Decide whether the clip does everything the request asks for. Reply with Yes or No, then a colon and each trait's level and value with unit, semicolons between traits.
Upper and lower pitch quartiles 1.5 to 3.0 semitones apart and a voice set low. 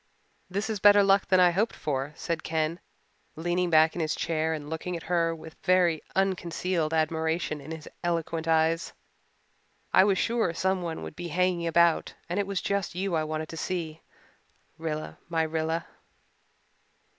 No: narrow, 2.4 semitones; medium, 165 Hz